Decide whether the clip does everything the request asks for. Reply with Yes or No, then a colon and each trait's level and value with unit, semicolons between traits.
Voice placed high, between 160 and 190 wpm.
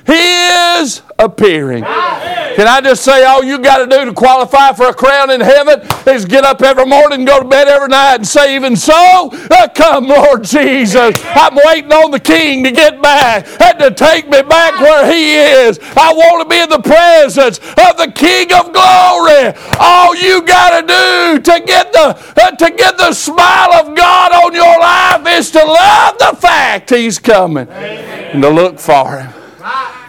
Yes: very high, 305 Hz; average, 185 wpm